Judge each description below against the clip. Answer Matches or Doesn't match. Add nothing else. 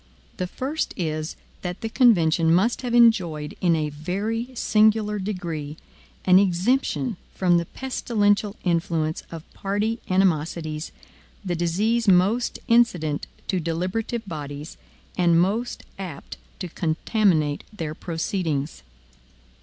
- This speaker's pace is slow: Matches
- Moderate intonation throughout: Matches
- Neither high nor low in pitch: Matches